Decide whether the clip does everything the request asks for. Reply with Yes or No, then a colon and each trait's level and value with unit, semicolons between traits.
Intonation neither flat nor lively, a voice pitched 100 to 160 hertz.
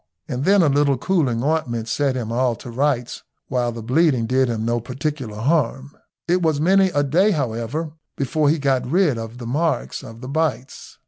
Yes: average, 4.7 semitones; low, 135 Hz